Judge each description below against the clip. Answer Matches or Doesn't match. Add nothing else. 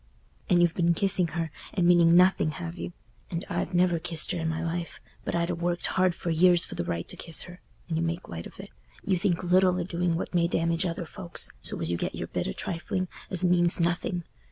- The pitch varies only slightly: Matches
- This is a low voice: Doesn't match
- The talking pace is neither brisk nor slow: Doesn't match